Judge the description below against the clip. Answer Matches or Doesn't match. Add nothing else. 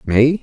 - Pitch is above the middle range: Doesn't match